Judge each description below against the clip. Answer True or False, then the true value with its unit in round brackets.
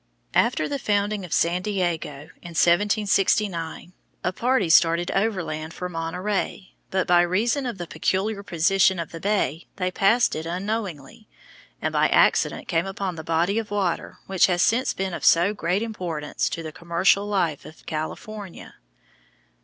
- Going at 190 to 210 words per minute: False (155 wpm)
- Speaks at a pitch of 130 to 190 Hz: True (185 Hz)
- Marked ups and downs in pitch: False (3.5 semitones)